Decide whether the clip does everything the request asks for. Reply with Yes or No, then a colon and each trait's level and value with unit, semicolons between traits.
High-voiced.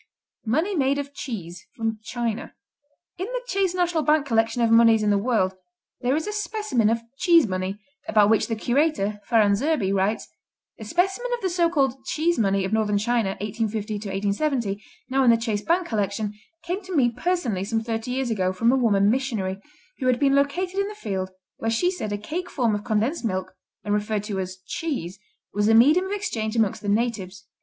Yes: high, 230 Hz